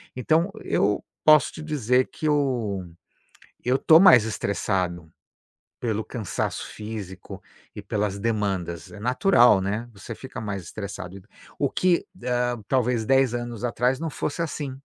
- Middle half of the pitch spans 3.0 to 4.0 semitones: No, average, 4.6 semitones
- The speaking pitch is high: No, low, 120 Hz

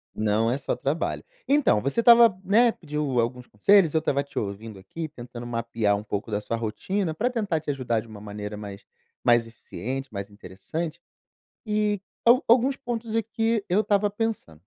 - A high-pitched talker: No, medium, 140 Hz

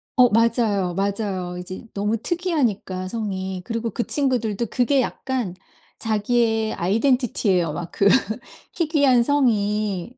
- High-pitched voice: Yes, high, 220 Hz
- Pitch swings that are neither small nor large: Yes, average, 4.3 semitones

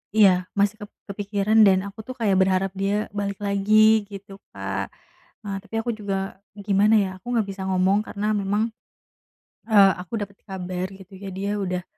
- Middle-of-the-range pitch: No, high, 200 Hz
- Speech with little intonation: Yes, narrow, 1.6 semitones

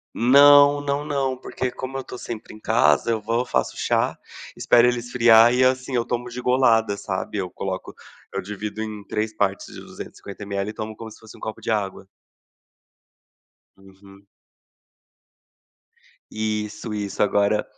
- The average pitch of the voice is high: No, low, 110 Hz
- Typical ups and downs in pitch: Yes, average, 3.3 semitones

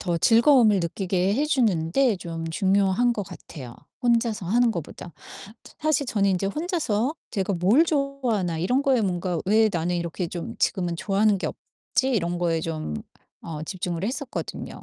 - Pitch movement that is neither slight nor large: No, wide, 5.9 semitones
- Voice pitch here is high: Yes, high, 195 Hz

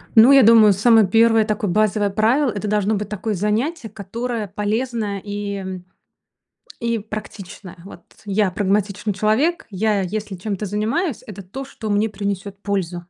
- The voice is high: Yes, high, 210 Hz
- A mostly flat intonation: Yes, narrow, 2.1 semitones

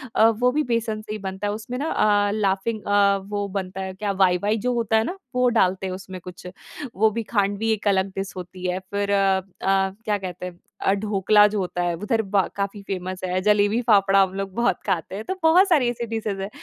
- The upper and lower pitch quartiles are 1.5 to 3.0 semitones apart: Yes, narrow, 2.5 semitones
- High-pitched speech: Yes, high, 200 Hz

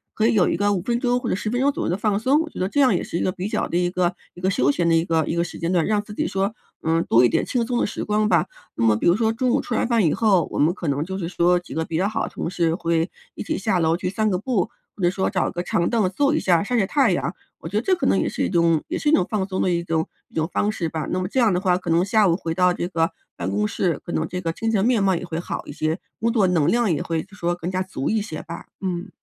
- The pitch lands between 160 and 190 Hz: Yes, medium, 185 Hz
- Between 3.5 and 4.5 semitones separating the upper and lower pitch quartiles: Yes, average, 4.2 semitones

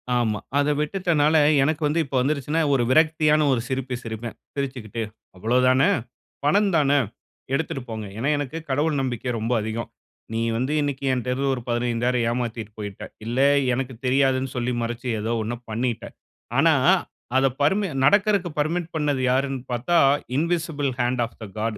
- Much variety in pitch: No, average, 3.8 semitones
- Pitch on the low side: Yes, low, 130 Hz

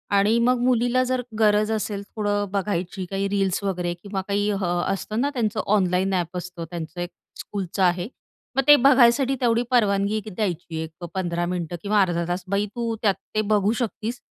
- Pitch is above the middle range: Yes, high, 200 Hz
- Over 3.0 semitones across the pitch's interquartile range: Yes, average, 3.6 semitones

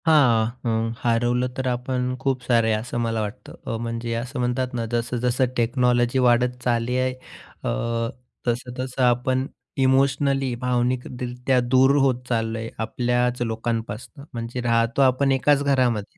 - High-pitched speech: No, low, 125 Hz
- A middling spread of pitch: No, narrow, 1.6 semitones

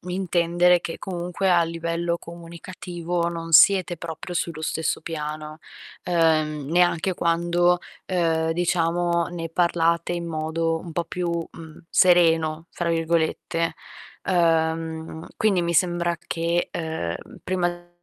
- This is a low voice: No, medium, 170 Hz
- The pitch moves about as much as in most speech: No, narrow, 1.2 semitones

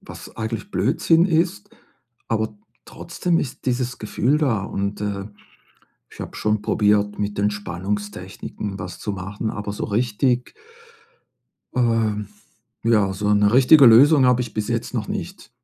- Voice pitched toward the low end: Yes, low, 110 Hz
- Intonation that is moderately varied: Yes, average, 3.6 semitones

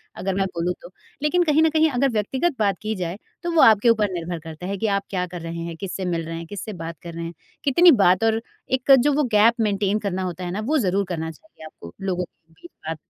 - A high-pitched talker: Yes, high, 195 Hz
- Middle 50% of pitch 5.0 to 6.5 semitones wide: Yes, wide, 5.4 semitones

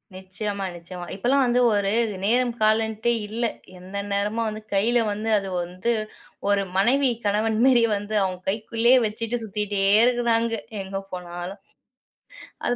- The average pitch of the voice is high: Yes, high, 215 Hz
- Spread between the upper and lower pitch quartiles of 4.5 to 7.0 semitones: No, average, 3.0 semitones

